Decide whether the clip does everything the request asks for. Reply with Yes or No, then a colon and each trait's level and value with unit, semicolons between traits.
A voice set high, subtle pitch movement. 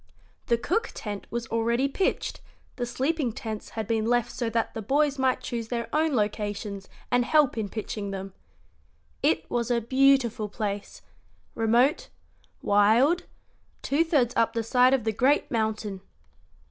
No: high, 235 Hz; average, 3.5 semitones